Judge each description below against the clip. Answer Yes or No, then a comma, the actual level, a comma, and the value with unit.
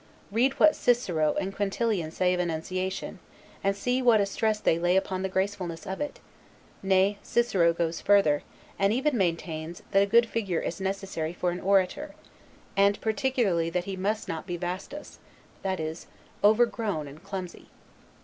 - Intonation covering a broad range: No, average, 3.3 semitones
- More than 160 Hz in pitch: Yes, high, 190 Hz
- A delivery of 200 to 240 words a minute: No, average, 160 wpm